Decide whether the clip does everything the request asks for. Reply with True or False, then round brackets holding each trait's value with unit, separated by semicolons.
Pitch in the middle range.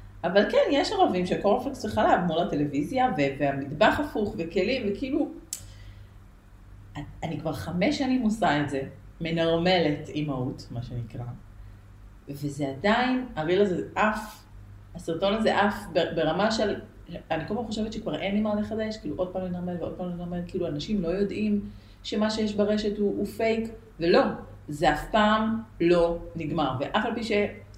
True (175 Hz)